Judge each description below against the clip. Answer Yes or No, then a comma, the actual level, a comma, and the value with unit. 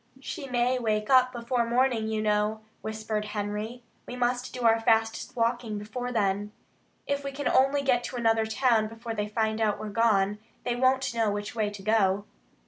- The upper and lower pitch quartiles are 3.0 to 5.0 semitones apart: No, narrow, 2.6 semitones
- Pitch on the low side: No, high, 225 Hz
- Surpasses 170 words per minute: Yes, average, 185 wpm